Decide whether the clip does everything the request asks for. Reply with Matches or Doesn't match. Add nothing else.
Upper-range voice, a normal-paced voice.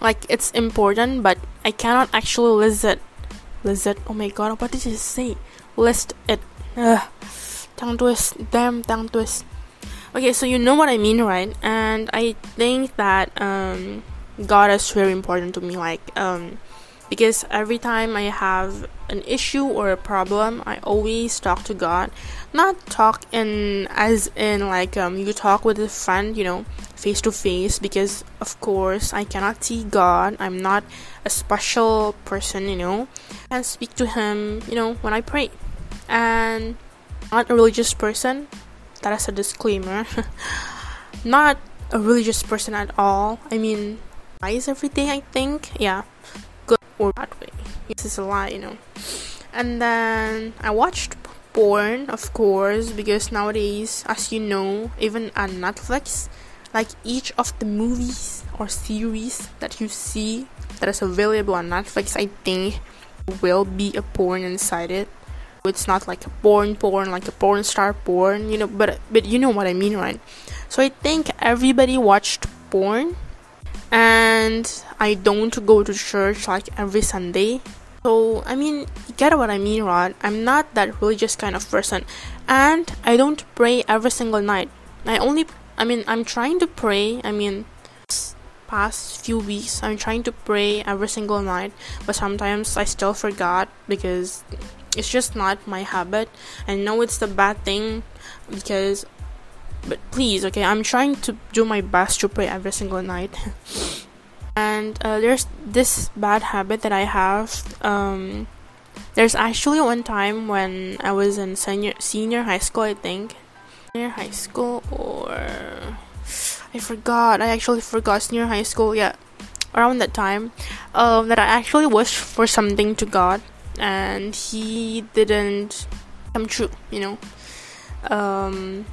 Doesn't match